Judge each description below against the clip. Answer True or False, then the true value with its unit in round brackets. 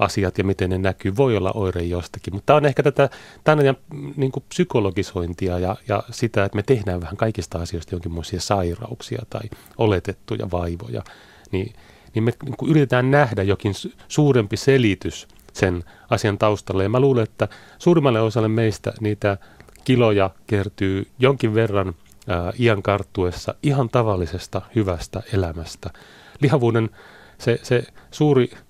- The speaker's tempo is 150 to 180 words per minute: False (140 wpm)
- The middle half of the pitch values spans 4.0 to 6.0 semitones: True (4.4 semitones)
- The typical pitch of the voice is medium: False (105 Hz)